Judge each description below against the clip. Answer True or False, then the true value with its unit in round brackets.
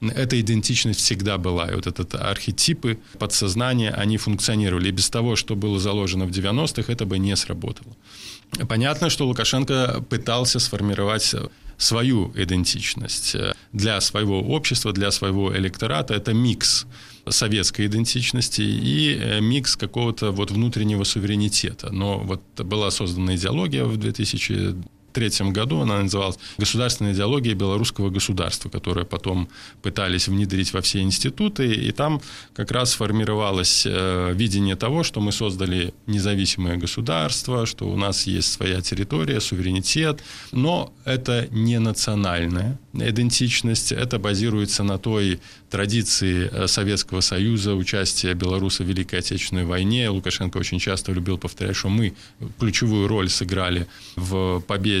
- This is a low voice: True (105 Hz)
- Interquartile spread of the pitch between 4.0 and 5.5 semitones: False (3.4 semitones)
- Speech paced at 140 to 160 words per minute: False (130 wpm)